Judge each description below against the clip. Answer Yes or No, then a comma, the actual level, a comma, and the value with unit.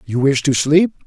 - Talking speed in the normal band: No, fast, 225 wpm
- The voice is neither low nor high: Yes, medium, 145 Hz